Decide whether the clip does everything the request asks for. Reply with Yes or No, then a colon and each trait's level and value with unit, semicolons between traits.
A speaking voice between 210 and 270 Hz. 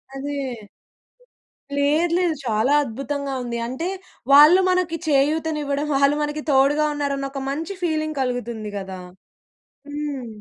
No: very high, 285 Hz